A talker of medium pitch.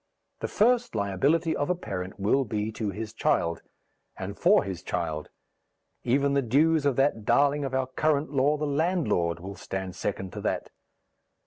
No: low, 130 Hz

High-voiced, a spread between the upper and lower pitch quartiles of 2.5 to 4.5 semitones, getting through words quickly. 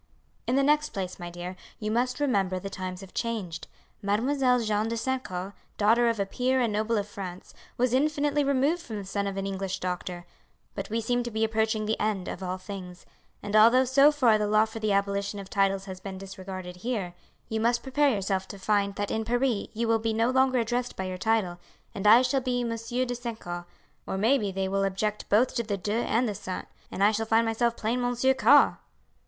Yes: high, 215 Hz; average, 3.8 semitones; fast, 225 wpm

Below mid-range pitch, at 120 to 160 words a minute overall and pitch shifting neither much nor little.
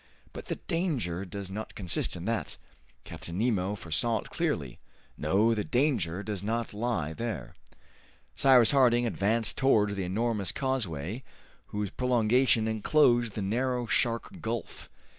Yes: low, 110 Hz; slow, 135 wpm; average, 3.8 semitones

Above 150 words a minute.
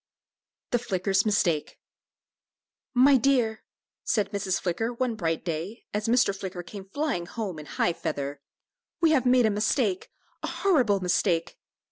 No: average, 140 wpm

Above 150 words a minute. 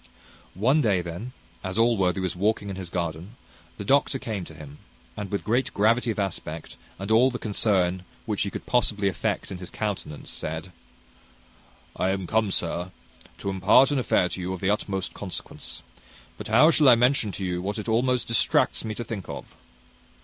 Yes: average, 185 wpm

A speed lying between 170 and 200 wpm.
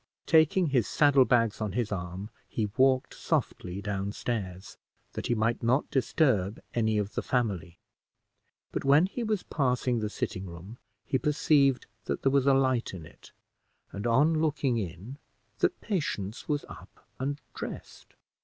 No: average, 155 wpm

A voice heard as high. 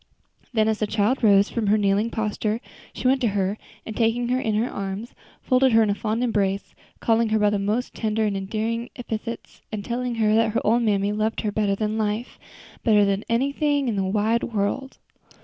Yes: high, 220 Hz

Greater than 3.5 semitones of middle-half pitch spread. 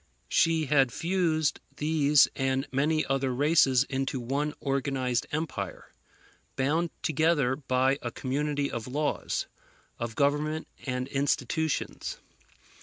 No: narrow, 2.6 semitones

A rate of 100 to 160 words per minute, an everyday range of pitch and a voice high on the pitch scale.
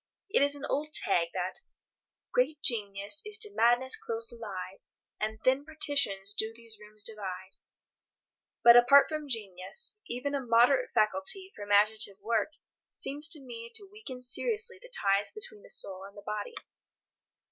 No: average, 155 wpm; wide, 6.8 semitones; high, 235 Hz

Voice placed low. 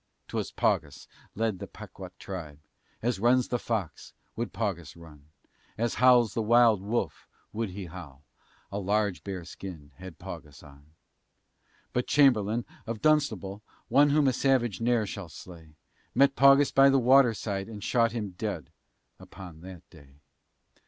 Yes: low, 105 Hz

